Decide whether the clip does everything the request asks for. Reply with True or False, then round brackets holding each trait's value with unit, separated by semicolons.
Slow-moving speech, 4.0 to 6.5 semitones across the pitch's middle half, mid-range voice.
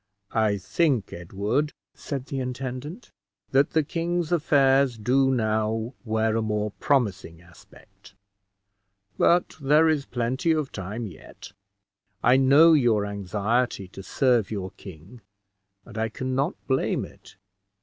False (130 wpm; 4.7 semitones; 125 Hz)